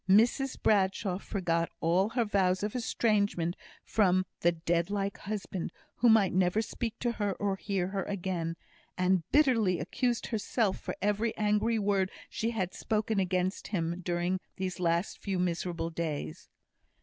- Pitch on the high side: Yes, high, 195 Hz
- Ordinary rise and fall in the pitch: Yes, average, 3.1 semitones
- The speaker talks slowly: No, average, 150 wpm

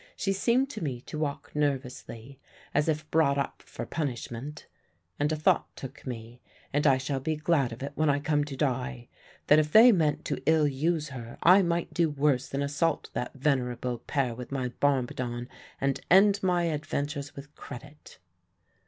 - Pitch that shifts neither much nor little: Yes, average, 3.1 semitones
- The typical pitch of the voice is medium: Yes, medium, 145 Hz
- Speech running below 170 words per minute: No, average, 180 wpm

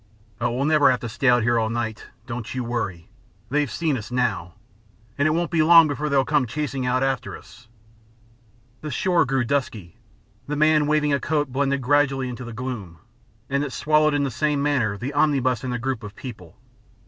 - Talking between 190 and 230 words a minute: Yes, average, 195 wpm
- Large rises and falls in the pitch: No, average, 3.7 semitones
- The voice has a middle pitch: No, low, 130 Hz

